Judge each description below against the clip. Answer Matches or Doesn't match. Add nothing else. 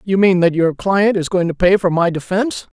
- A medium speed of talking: Doesn't match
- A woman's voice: Doesn't match